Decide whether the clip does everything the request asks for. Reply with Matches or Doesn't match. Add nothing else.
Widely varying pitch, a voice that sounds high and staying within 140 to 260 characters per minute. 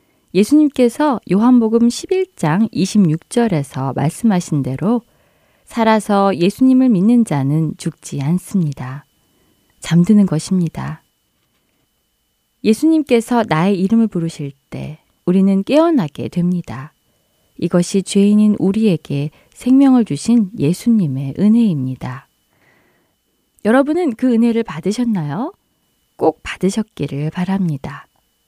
Matches